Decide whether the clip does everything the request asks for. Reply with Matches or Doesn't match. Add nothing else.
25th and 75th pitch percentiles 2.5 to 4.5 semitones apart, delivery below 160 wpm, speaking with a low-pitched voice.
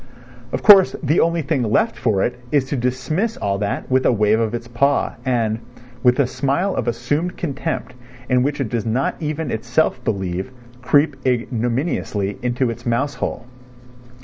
Doesn't match